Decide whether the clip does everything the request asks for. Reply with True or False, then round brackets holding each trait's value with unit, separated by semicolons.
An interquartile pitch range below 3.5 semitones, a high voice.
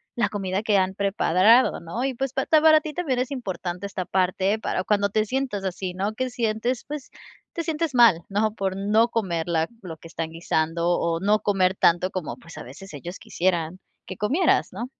False (5.0 semitones; 200 Hz)